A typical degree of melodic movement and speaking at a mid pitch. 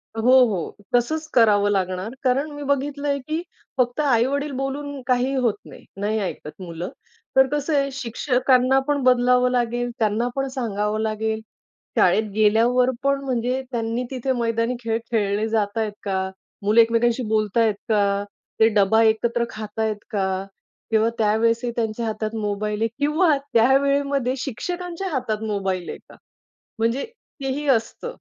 No: average, 3.7 semitones; high, 230 Hz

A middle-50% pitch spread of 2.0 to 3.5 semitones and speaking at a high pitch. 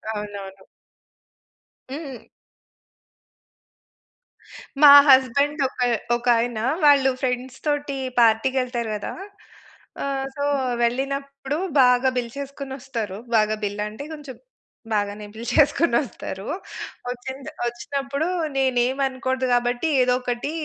Yes: average, 2.8 semitones; very high, 255 Hz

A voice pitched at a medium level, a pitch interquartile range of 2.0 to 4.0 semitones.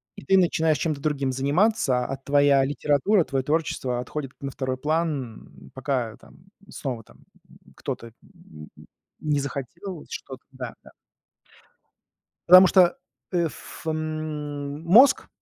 Yes: medium, 145 Hz; average, 3.5 semitones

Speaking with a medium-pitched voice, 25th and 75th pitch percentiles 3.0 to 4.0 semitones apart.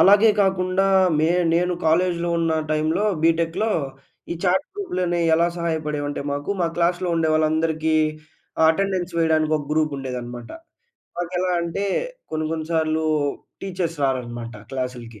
No: medium, 165 Hz; narrow, 2.6 semitones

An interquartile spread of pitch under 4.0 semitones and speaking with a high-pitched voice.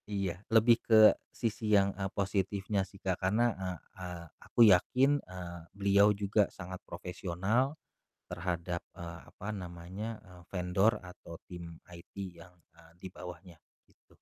No: narrow, 2.5 semitones; very low, 95 Hz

